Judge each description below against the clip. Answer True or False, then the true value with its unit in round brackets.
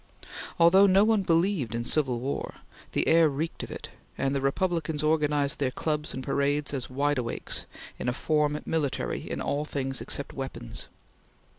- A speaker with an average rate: True (165 wpm)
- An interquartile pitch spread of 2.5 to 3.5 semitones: True (3.0 semitones)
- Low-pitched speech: False (145 Hz)